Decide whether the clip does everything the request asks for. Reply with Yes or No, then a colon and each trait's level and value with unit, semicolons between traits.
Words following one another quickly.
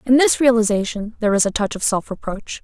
Yes: fast, 230 wpm